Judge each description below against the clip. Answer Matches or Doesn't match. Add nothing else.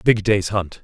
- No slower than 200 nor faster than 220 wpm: Matches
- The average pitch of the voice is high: Doesn't match